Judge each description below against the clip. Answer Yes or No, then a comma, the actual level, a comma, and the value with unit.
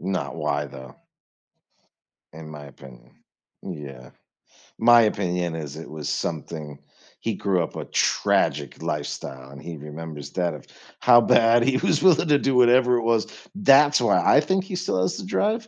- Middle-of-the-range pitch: No, very low, 90 Hz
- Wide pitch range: Yes, wide, 8.9 semitones